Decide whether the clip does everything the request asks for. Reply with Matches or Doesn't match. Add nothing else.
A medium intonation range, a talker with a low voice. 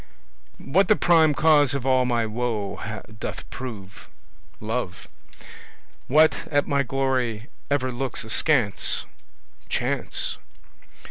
Matches